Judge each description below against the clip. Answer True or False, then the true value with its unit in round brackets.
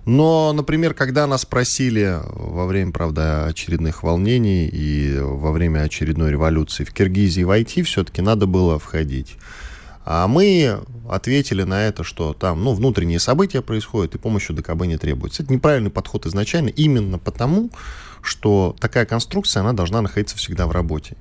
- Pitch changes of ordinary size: False (6.8 semitones)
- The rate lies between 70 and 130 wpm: False (150 wpm)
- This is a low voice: True (100 Hz)